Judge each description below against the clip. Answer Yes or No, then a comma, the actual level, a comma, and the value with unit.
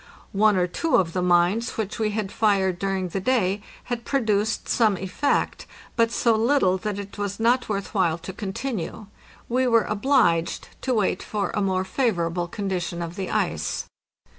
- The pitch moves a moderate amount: Yes, average, 3.5 semitones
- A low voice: No, high, 200 Hz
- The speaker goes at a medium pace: Yes, average, 170 wpm